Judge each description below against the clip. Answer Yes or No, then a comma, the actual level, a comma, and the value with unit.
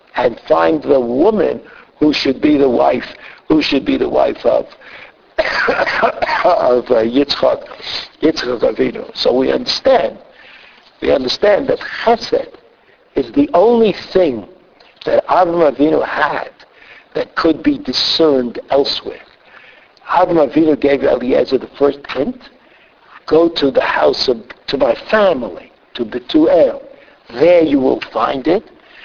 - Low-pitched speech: No, medium, 175 Hz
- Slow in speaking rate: Yes, slow, 125 wpm